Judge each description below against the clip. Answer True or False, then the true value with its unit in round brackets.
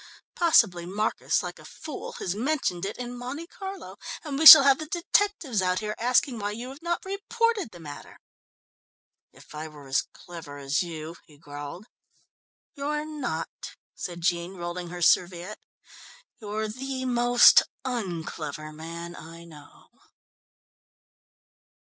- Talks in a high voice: True (205 Hz)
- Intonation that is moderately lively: False (8.3 semitones)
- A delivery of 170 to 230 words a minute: False (140 wpm)